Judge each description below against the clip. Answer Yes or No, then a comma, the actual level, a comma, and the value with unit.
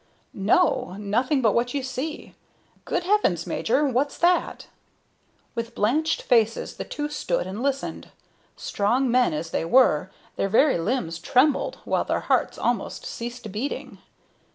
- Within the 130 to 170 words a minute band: Yes, average, 140 wpm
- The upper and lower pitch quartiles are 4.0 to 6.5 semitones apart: Yes, average, 5.3 semitones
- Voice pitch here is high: Yes, high, 245 Hz